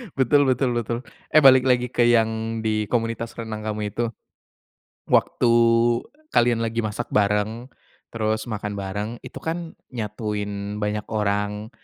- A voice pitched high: No, low, 110 Hz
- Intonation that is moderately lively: No, narrow, 2.2 semitones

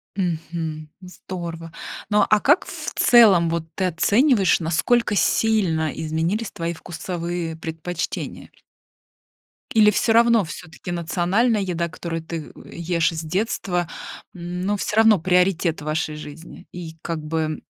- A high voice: No, medium, 175 Hz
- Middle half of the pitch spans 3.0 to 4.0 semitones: Yes, average, 3.5 semitones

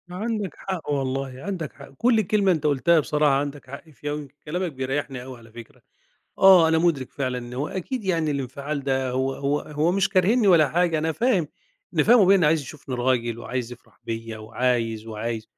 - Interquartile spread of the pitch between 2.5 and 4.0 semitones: No, average, 5.2 semitones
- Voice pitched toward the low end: No, medium, 145 Hz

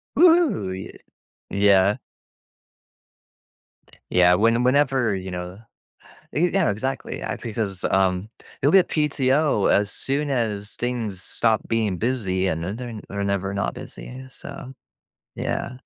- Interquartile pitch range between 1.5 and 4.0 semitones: No, average, 5.3 semitones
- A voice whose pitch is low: Yes, low, 110 Hz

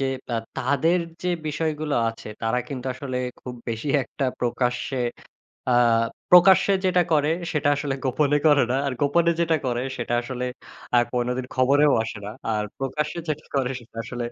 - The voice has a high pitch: No, low, 135 Hz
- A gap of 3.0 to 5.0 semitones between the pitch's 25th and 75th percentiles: Yes, average, 3.4 semitones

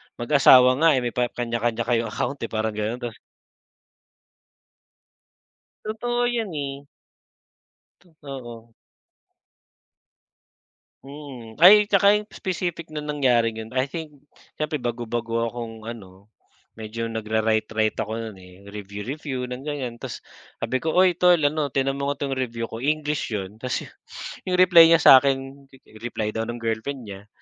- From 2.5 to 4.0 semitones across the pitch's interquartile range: No, average, 4.7 semitones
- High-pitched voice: No, low, 125 Hz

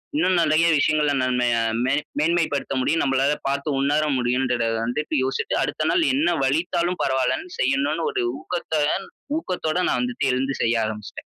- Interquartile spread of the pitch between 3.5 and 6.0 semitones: Yes, average, 4.2 semitones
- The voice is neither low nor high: Yes, medium, 145 Hz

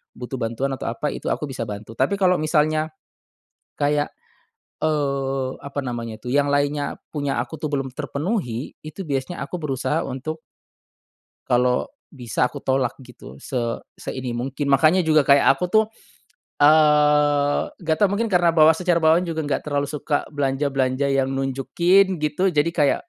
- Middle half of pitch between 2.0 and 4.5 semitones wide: Yes, average, 2.8 semitones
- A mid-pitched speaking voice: Yes, medium, 145 Hz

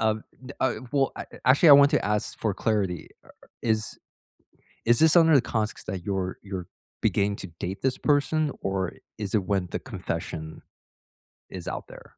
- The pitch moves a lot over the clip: Yes, wide, 6.1 semitones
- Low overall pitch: Yes, low, 105 Hz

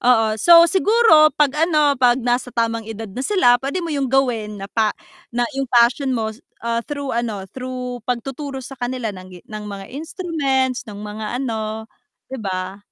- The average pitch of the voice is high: Yes, high, 245 Hz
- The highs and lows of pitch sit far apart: No, average, 3.7 semitones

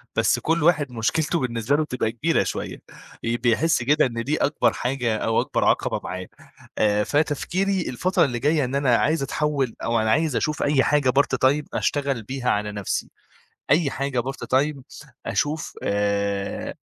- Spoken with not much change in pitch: No, average, 4.5 semitones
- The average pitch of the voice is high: No, low, 135 Hz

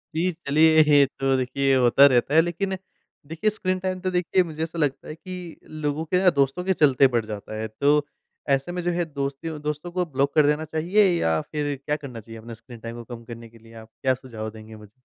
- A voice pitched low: No, medium, 145 Hz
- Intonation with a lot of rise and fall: Yes, wide, 5.8 semitones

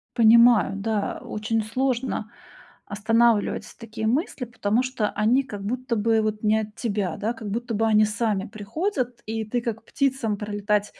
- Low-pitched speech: No, high, 225 Hz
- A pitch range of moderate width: No, narrow, 2.2 semitones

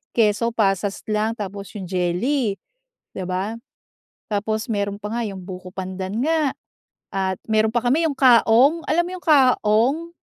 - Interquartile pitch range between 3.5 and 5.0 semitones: Yes, average, 4.7 semitones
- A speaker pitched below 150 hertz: No, high, 215 Hz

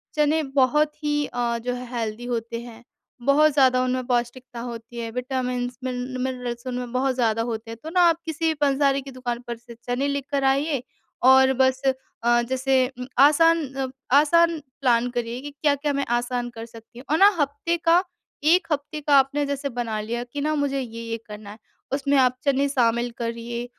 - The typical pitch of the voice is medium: No, very high, 255 Hz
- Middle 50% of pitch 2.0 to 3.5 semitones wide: Yes, average, 3.0 semitones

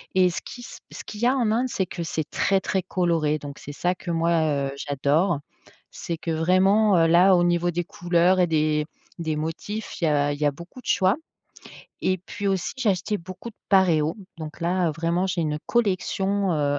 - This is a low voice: No, medium, 175 Hz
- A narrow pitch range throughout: No, average, 3.2 semitones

